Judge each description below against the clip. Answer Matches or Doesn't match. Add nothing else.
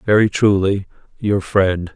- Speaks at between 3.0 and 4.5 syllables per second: Matches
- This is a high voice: Doesn't match